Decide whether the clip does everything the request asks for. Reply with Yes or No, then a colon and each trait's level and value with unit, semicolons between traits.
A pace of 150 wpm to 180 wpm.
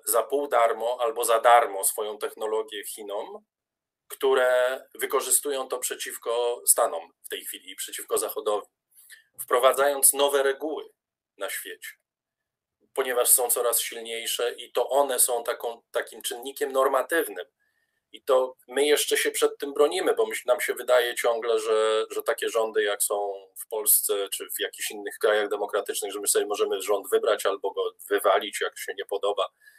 Yes: average, 155 wpm